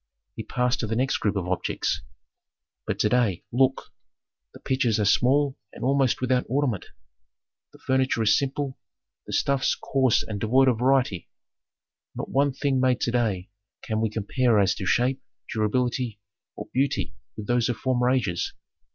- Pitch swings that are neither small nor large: Yes, average, 3.3 semitones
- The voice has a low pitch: Yes, low, 125 Hz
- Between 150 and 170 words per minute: Yes, average, 160 wpm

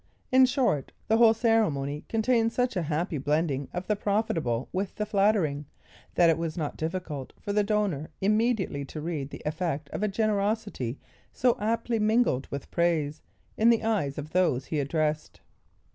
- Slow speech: No, average, 165 wpm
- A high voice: No, medium, 180 Hz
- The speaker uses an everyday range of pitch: No, wide, 6.5 semitones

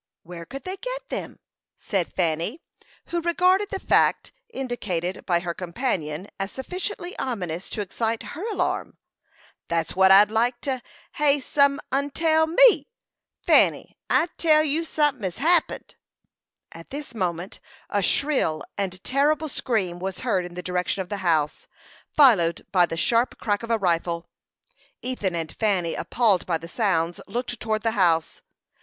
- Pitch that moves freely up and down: Yes, wide, 8.0 semitones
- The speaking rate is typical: Yes, average, 155 wpm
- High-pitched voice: Yes, high, 215 Hz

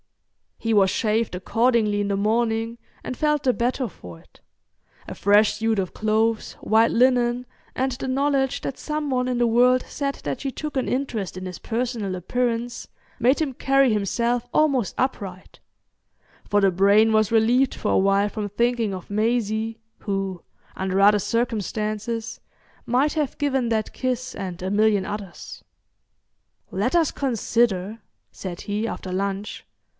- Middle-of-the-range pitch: No, high, 225 Hz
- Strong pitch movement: No, average, 3.7 semitones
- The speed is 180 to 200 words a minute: No, average, 155 wpm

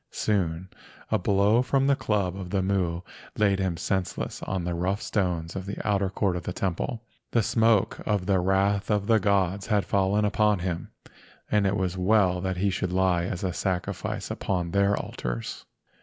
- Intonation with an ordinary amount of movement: No, narrow, 2.2 semitones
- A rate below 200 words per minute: Yes, average, 185 wpm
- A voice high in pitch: No, very low, 95 Hz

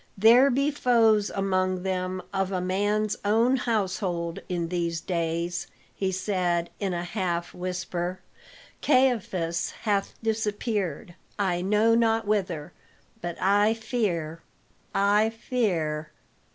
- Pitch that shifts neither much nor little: Yes, average, 3.8 semitones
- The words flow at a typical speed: No, slow, 110 wpm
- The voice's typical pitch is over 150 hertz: Yes, high, 190 Hz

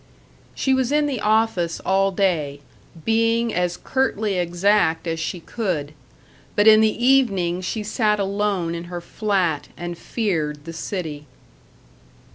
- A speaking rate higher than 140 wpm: No, slow, 135 wpm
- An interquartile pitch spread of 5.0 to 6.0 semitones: No, average, 4.4 semitones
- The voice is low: No, high, 195 Hz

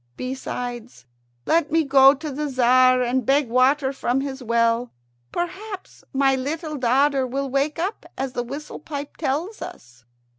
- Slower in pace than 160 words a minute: Yes, average, 150 wpm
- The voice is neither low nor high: No, very high, 270 Hz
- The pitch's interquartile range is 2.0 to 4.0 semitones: Yes, average, 2.8 semitones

